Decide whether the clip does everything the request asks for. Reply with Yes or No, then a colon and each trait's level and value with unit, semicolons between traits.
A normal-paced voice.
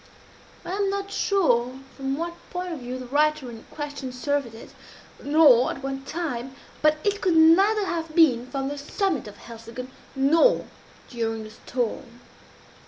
Yes: average, 160 wpm